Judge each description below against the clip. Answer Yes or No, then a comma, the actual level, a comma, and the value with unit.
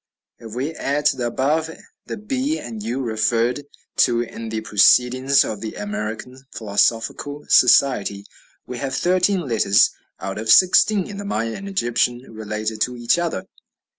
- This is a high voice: No, low, 120 Hz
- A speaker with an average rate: Yes, average, 155 wpm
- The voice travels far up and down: No, average, 4.9 semitones